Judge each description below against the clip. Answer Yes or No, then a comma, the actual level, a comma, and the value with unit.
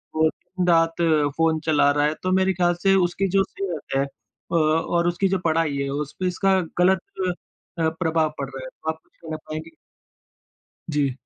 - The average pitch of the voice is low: No, medium, 160 Hz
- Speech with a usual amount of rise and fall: Yes, average, 3.1 semitones